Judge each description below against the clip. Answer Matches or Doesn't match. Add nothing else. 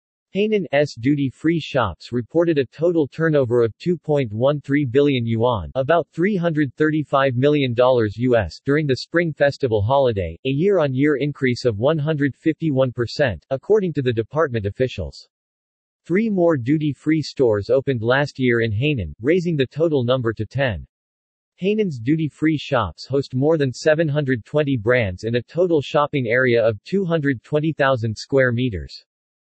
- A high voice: Doesn't match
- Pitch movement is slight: Doesn't match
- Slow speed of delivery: Matches